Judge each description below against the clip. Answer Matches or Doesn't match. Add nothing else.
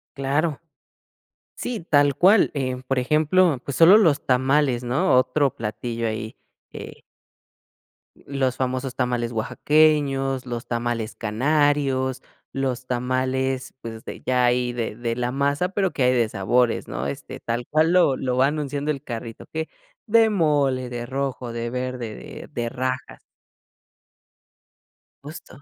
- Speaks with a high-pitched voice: Doesn't match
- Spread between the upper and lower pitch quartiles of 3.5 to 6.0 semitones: Doesn't match